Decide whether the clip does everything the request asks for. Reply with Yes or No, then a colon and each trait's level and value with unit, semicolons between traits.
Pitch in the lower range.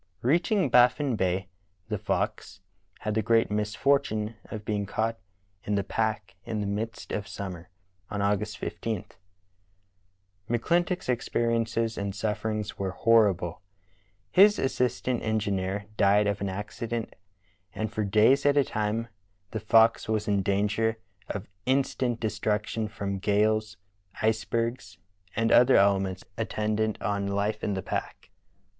Yes: low, 110 Hz